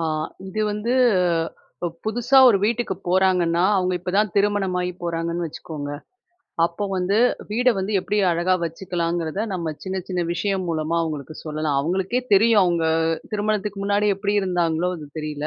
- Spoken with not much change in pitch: No, average, 3.5 semitones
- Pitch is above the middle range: No, medium, 180 Hz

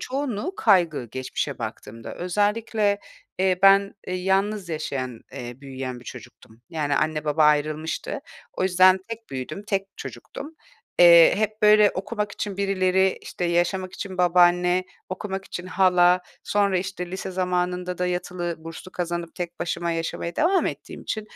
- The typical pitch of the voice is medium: Yes, medium, 180 Hz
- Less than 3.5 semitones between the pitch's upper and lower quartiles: Yes, average, 3.1 semitones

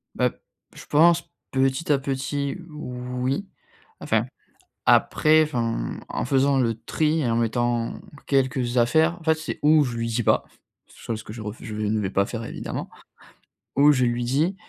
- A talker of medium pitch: No, low, 130 Hz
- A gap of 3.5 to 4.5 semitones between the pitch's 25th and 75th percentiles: Yes, average, 4.1 semitones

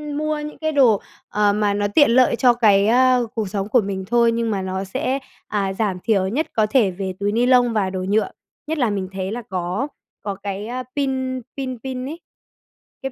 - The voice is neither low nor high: No, high, 220 Hz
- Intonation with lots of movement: No, average, 4.5 semitones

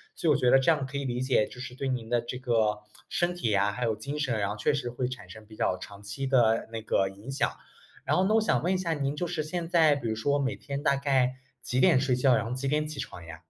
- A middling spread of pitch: Yes, average, 4.1 semitones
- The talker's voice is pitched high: No, low, 130 Hz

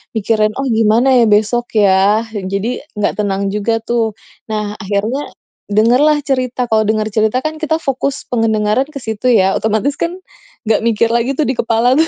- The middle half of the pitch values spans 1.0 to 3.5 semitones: Yes, average, 3.2 semitones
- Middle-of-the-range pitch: No, high, 225 Hz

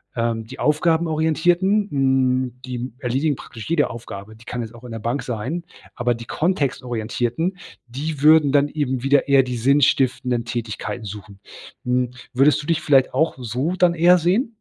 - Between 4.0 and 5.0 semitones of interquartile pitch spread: Yes, average, 4.7 semitones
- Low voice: Yes, low, 130 Hz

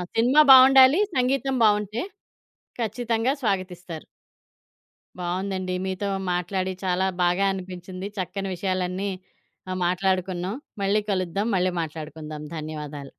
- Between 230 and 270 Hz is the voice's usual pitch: No, medium, 185 Hz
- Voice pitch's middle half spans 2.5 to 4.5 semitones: Yes, average, 2.8 semitones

